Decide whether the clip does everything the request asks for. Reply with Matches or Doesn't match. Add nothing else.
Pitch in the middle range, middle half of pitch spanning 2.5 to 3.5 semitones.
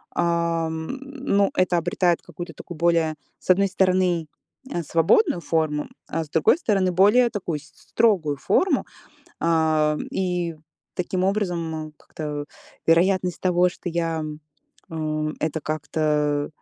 Matches